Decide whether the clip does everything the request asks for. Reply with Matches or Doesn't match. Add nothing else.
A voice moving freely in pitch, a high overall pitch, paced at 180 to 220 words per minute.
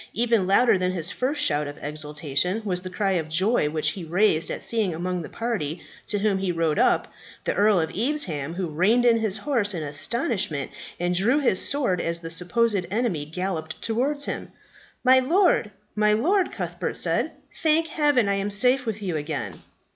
Matches